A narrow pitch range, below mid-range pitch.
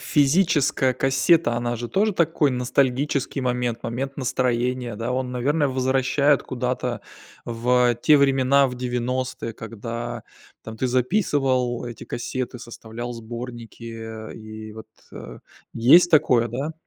Yes: narrow, 2.3 semitones; low, 125 Hz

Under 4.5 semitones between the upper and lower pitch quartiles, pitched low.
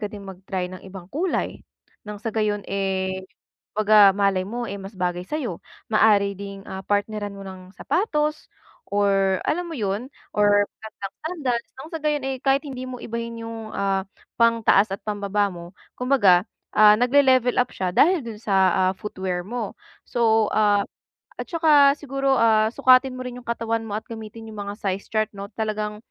No: average, 3.9 semitones; high, 215 Hz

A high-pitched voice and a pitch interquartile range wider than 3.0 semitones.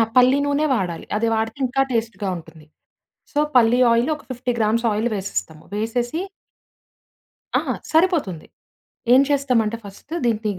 Yes: high, 230 Hz; average, 3.6 semitones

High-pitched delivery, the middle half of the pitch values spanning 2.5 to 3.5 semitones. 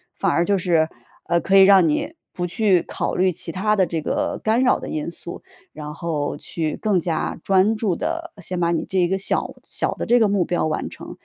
No: medium, 180 Hz; average, 3.2 semitones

